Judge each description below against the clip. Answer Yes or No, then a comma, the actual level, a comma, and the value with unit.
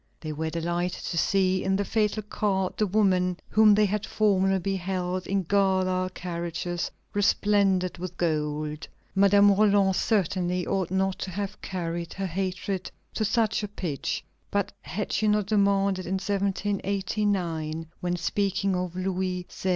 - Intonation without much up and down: Yes, narrow, 2.1 semitones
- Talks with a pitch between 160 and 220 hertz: Yes, high, 190 Hz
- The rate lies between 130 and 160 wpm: Yes, average, 145 wpm